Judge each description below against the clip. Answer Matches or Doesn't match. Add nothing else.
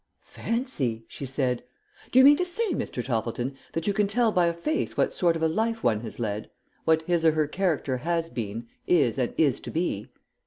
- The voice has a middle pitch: Matches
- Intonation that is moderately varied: Doesn't match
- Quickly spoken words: Matches